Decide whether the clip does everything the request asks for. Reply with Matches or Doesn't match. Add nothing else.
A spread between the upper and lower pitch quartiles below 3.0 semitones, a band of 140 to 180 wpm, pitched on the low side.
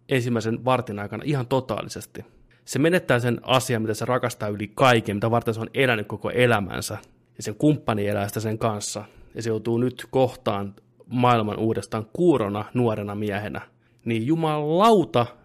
Matches